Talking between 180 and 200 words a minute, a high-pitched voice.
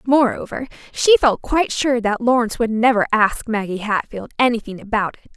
No: average, 170 wpm; high, 230 Hz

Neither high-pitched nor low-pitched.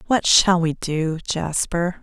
Yes: medium, 170 Hz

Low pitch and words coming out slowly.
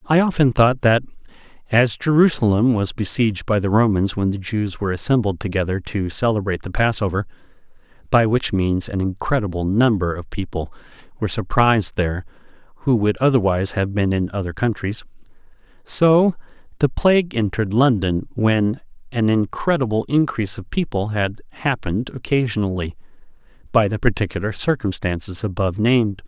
Yes: low, 110 Hz; slow, 130 wpm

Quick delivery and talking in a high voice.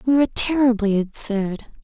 No: slow, 130 wpm; high, 230 Hz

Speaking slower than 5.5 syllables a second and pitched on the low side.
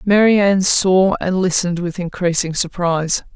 No: 4.8 syllables/s; medium, 180 Hz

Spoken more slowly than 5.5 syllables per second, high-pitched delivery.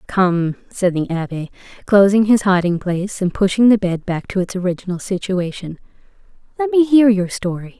Yes: 5.2 syllables/s; high, 195 Hz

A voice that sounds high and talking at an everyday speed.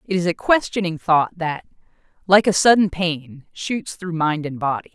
No: medium, 175 Hz; average, 180 wpm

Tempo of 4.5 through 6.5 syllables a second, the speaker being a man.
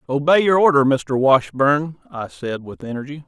Yes: 4.7 syllables/s; male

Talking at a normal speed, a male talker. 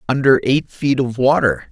Yes: average, 175 wpm; male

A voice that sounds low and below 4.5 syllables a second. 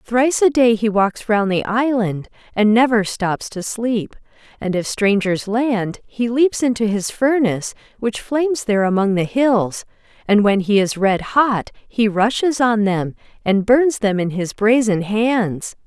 No: high, 220 Hz; 4.1 syllables/s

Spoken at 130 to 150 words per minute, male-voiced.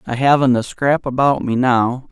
No: average, 200 wpm; male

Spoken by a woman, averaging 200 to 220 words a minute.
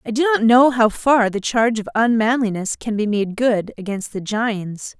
Yes: female; fast, 205 wpm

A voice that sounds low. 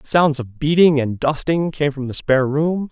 No: medium, 145 Hz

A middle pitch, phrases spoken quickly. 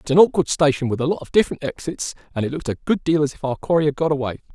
Yes: medium, 145 Hz; fast, 315 wpm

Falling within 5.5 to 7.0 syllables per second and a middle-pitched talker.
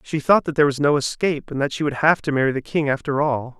Yes: 6.6 syllables/s; medium, 145 Hz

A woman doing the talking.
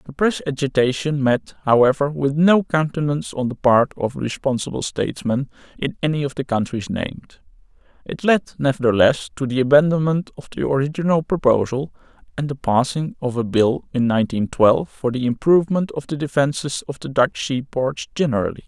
No: male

